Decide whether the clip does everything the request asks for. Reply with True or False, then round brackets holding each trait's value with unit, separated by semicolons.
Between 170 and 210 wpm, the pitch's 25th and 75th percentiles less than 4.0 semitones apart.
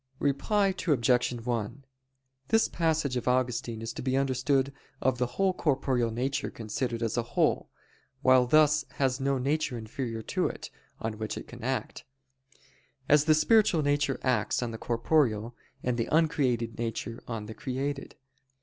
False (155 wpm; 3.5 semitones)